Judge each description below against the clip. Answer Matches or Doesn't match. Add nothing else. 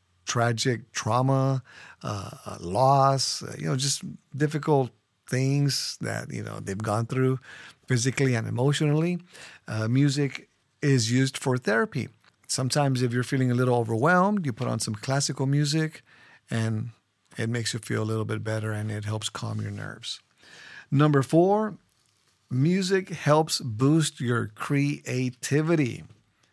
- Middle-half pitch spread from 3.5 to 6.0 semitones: Matches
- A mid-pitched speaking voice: Doesn't match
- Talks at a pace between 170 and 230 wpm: Doesn't match